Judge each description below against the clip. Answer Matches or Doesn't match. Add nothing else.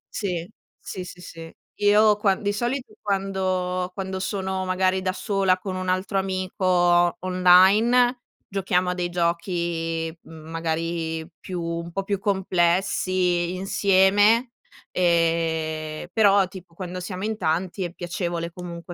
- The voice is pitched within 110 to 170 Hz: Doesn't match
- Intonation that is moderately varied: Doesn't match